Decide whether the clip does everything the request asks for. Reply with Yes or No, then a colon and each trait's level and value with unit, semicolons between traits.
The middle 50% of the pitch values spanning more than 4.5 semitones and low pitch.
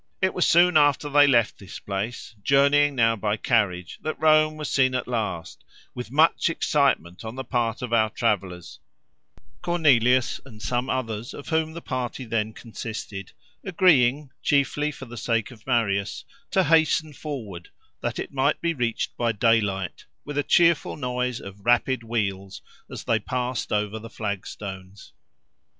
Yes: average, 5.2 semitones; low, 125 Hz